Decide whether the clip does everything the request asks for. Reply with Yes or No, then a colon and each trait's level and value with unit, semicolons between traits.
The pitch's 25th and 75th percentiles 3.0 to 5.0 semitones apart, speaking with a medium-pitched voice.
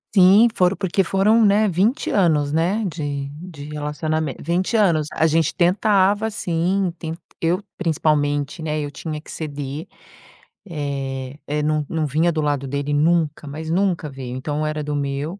Yes: average, 3.8 semitones; medium, 155 Hz